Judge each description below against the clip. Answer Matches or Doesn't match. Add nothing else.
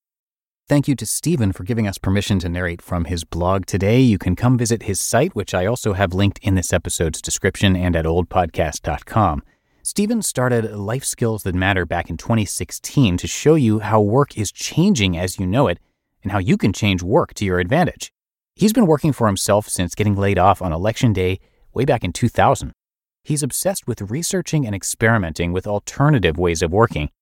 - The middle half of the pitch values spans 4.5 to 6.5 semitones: Matches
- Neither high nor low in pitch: Doesn't match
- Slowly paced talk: Doesn't match